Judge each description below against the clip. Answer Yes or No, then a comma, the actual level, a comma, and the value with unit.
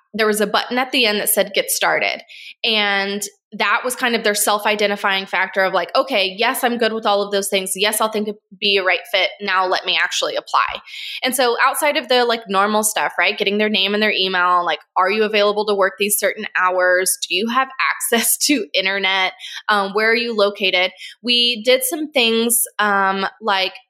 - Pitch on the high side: Yes, high, 210 Hz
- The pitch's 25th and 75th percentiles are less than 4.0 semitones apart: Yes, average, 3.5 semitones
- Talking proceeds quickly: Yes, fast, 215 wpm